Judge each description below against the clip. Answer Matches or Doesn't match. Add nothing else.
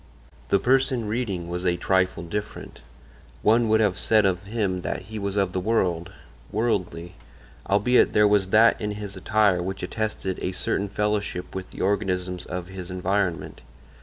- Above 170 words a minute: Doesn't match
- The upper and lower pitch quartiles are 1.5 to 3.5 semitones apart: Matches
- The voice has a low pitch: Matches